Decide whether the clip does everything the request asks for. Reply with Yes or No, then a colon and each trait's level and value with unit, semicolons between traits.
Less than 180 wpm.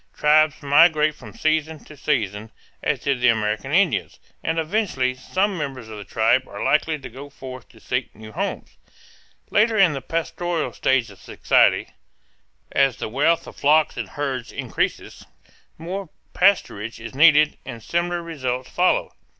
Yes: average, 155 wpm